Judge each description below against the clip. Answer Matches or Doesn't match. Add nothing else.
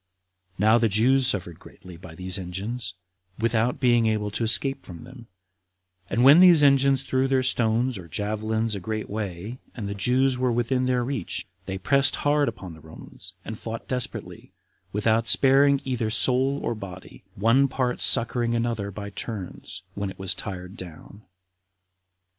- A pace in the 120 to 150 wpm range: Doesn't match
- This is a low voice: Matches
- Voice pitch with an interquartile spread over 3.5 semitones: Matches